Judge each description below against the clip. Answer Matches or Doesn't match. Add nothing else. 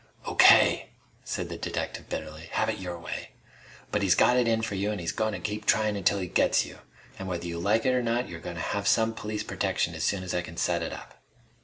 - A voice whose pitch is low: Matches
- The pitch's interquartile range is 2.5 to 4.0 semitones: Matches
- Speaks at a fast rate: Matches